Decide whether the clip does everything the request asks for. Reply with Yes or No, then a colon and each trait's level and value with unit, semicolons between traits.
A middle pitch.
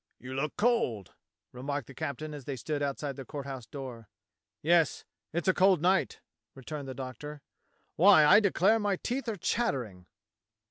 Yes: medium, 145 Hz